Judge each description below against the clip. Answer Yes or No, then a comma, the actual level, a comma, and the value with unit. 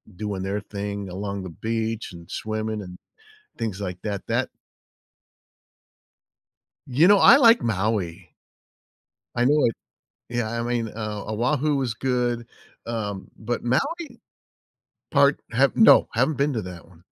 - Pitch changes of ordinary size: Yes, average, 3.3 semitones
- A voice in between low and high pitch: No, low, 110 Hz